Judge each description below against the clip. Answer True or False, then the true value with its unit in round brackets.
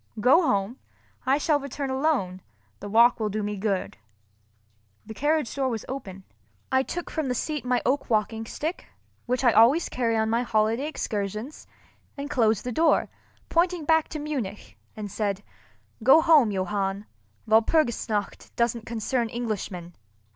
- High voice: True (235 Hz)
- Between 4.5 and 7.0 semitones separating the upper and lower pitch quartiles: True (5.0 semitones)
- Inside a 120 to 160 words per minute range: True (145 wpm)